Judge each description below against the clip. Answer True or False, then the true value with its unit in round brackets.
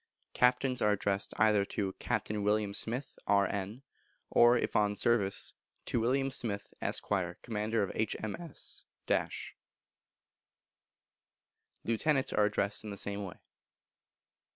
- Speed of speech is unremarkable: False (115 wpm)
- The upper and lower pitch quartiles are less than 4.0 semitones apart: True (2.9 semitones)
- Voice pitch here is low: True (105 Hz)